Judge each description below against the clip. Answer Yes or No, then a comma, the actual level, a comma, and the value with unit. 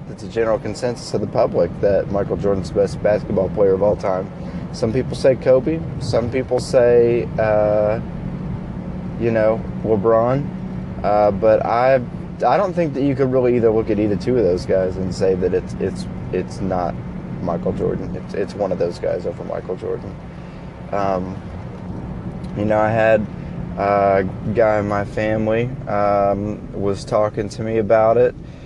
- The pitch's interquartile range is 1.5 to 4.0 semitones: Yes, average, 3.7 semitones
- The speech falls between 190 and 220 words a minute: No, average, 170 wpm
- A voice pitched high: No, low, 110 Hz